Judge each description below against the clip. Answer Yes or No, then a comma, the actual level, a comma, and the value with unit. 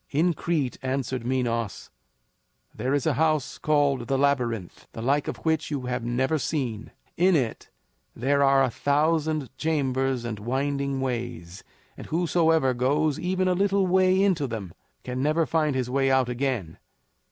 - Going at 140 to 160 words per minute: Yes, average, 155 wpm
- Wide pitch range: No, average, 3.8 semitones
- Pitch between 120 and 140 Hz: Yes, low, 135 Hz